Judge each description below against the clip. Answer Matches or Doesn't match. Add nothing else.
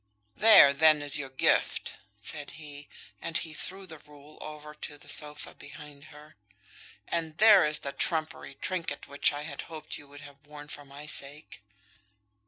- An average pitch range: Doesn't match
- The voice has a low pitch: Doesn't match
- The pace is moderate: Matches